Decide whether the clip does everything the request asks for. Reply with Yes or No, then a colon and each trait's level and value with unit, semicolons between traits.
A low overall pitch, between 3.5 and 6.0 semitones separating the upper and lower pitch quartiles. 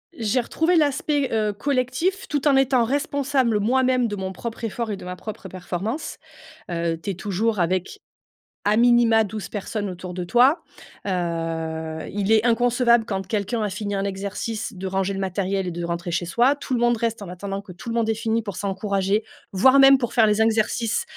No: high, 215 Hz; average, 4.0 semitones